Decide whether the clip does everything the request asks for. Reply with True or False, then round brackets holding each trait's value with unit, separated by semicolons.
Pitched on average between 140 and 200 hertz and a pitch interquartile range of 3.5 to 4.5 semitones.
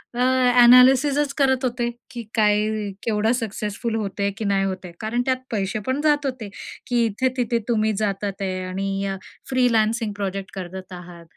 False (220 Hz; 4.1 semitones)